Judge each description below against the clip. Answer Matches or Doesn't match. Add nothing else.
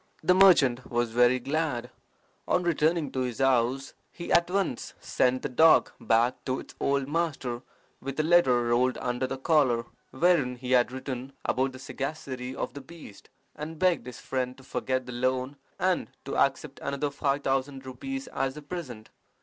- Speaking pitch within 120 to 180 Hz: Matches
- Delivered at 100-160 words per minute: Doesn't match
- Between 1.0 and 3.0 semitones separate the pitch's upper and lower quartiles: Doesn't match